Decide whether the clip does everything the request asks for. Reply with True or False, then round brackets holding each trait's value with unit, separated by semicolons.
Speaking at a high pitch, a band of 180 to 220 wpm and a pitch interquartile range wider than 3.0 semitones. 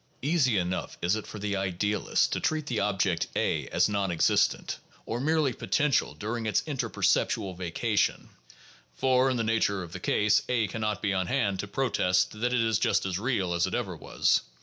False (105 Hz; 195 wpm; 4.4 semitones)